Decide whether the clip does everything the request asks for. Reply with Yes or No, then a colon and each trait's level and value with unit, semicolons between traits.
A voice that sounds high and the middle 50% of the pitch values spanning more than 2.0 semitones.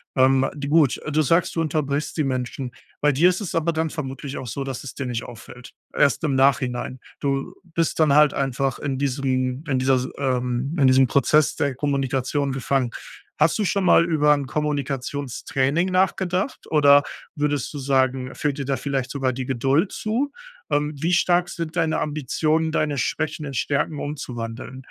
No: medium, 140 Hz; average, 2.8 semitones